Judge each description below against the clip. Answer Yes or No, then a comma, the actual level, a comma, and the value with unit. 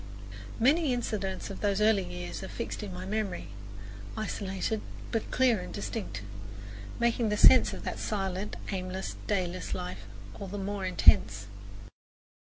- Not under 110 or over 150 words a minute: Yes, average, 140 wpm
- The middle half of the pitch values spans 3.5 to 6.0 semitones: No, average, 2.9 semitones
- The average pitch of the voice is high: Yes, high, 195 Hz